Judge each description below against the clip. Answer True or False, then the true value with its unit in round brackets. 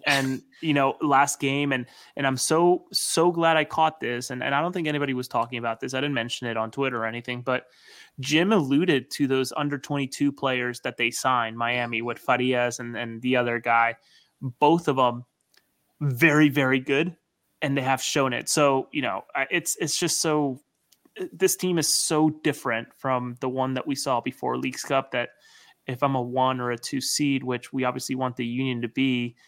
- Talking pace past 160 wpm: True (205 wpm)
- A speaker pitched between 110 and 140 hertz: True (135 Hz)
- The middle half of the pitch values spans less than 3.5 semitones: True (3.0 semitones)